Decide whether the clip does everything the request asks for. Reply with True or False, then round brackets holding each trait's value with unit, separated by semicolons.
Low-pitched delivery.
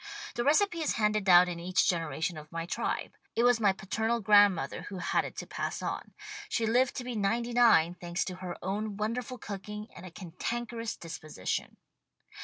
False (205 Hz)